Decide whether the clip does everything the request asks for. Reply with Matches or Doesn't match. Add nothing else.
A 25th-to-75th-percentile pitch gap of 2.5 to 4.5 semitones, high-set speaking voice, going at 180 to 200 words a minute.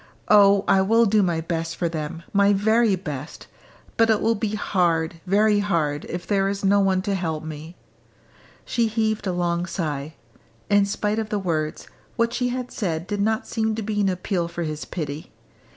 Matches